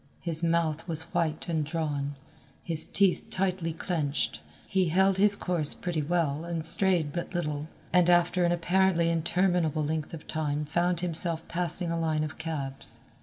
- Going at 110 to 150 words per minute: No, average, 160 wpm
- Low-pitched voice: No, medium, 165 Hz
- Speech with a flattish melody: Yes, narrow, 2.3 semitones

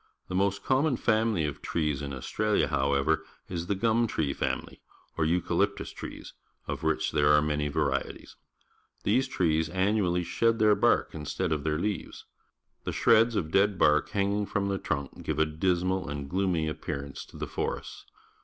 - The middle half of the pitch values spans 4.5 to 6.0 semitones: Yes, average, 4.9 semitones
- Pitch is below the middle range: Yes, very low, 85 Hz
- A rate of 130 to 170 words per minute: Yes, average, 165 wpm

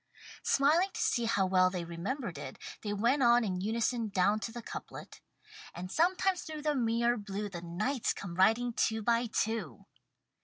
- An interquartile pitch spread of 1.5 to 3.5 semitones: No, average, 4.4 semitones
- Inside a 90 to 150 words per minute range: No, average, 170 wpm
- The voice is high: Yes, high, 225 Hz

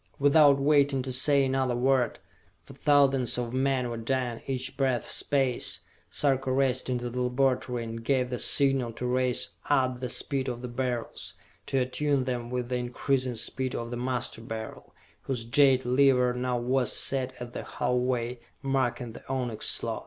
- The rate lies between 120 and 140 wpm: No, average, 170 wpm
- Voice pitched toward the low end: Yes, low, 125 Hz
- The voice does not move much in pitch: Yes, narrow, 1.7 semitones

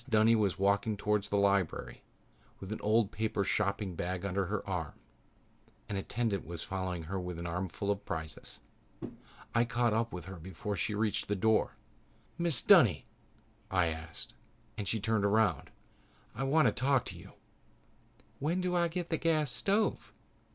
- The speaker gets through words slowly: No, average, 165 wpm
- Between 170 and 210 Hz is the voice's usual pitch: No, low, 105 Hz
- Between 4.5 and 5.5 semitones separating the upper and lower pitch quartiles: No, average, 3.7 semitones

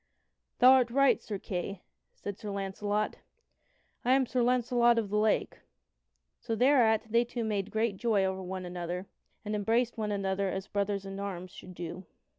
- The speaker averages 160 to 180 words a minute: Yes, average, 175 wpm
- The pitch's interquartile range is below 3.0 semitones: No, average, 3.5 semitones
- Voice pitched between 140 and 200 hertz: No, high, 210 Hz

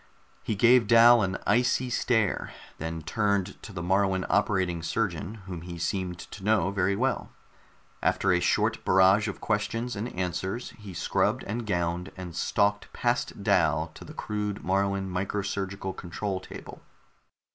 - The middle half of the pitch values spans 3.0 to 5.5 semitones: No, narrow, 2.5 semitones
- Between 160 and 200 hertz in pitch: No, low, 100 Hz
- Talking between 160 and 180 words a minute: No, average, 150 wpm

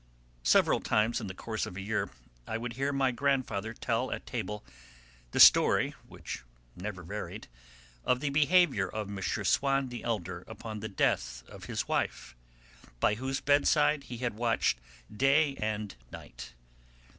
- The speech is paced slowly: No, average, 155 wpm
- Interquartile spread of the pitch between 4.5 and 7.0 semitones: Yes, average, 4.8 semitones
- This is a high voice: No, low, 115 Hz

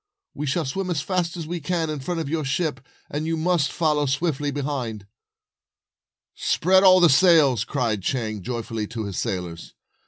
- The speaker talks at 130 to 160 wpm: No, average, 175 wpm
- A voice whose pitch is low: No, medium, 145 Hz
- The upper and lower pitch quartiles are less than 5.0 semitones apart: No, wide, 5.5 semitones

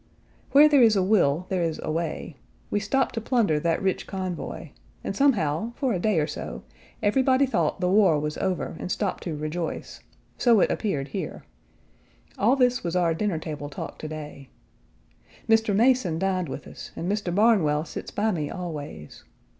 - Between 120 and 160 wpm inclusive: No, average, 180 wpm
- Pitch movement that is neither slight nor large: No, wide, 5.7 semitones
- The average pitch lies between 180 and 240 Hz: Yes, medium, 185 Hz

